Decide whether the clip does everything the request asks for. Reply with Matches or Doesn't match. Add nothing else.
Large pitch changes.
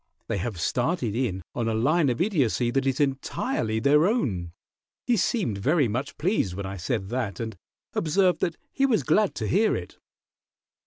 Matches